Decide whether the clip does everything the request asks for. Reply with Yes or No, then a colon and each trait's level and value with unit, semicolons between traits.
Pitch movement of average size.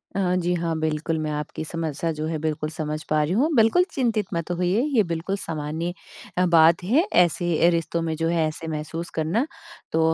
No: narrow, 2.2 semitones